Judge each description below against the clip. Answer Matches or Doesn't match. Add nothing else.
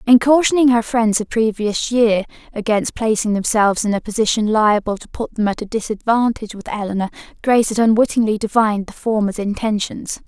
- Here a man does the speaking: Doesn't match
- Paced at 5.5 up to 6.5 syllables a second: Matches